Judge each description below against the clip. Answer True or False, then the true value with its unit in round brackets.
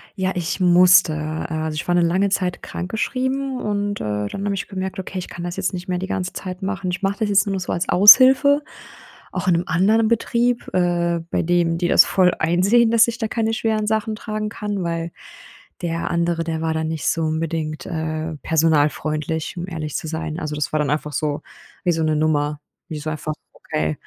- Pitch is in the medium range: True (175 Hz)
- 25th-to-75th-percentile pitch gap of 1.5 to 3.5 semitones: False (4.0 semitones)